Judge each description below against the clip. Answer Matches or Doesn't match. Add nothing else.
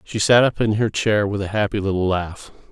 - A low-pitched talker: Matches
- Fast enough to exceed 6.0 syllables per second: Doesn't match